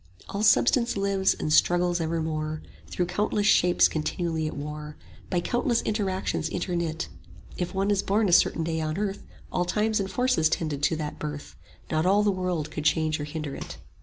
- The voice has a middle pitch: Yes, medium, 175 Hz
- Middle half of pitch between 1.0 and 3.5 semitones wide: No, average, 4.1 semitones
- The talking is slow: No, average, 185 wpm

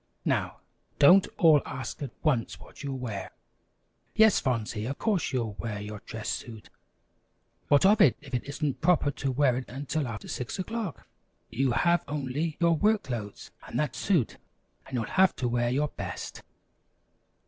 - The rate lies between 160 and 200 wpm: Yes, average, 165 wpm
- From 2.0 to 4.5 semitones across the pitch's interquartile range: No, average, 5.3 semitones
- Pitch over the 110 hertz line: Yes, medium, 140 Hz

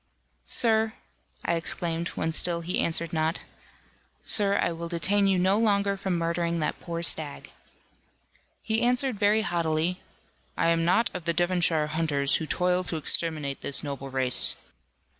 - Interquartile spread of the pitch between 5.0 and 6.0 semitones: No, average, 3.2 semitones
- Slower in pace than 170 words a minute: Yes, average, 150 wpm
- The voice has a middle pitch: Yes, medium, 170 Hz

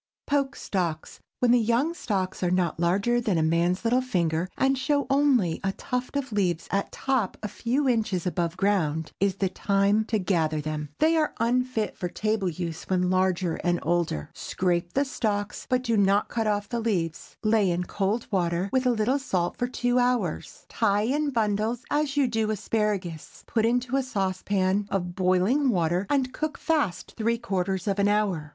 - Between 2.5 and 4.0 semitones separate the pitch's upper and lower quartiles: No, average, 5.2 semitones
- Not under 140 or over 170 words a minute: No, average, 185 wpm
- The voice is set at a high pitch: Yes, high, 205 Hz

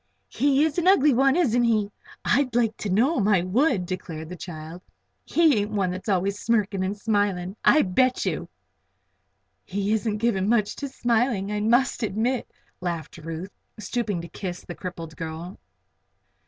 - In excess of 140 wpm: Yes, average, 165 wpm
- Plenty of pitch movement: No, average, 4.8 semitones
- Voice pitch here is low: No, high, 205 Hz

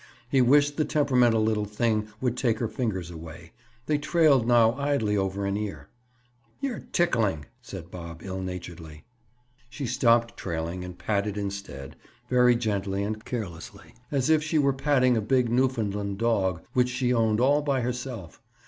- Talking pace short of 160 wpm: Yes, average, 150 wpm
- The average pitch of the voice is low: Yes, low, 115 Hz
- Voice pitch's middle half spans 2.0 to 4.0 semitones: No, average, 4.7 semitones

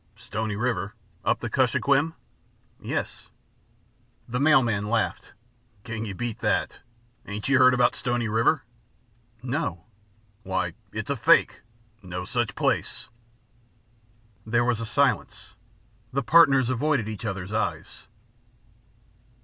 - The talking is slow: Yes, slow, 115 wpm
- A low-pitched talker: Yes, low, 115 Hz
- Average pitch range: Yes, average, 3.6 semitones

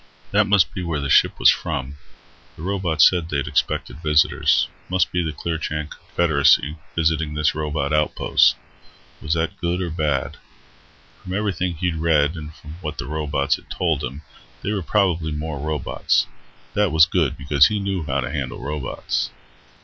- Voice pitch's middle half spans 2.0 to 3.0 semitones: Yes, average, 2.7 semitones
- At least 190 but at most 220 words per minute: No, average, 165 wpm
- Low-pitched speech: Yes, very low, 80 Hz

